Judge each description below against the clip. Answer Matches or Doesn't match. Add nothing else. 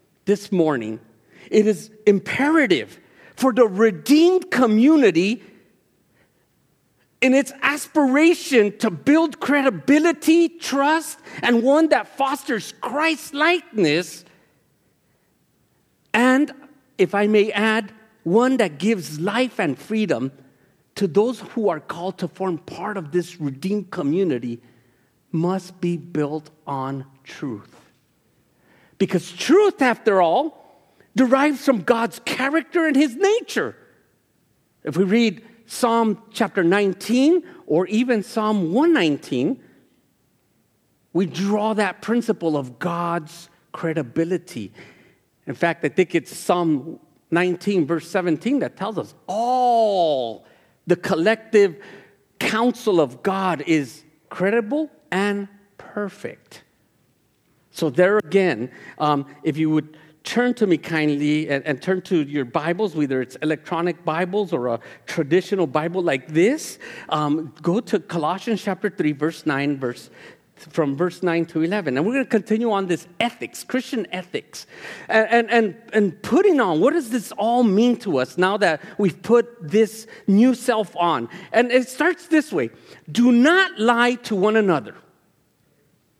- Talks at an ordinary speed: Doesn't match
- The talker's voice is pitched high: Matches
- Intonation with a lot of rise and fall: Matches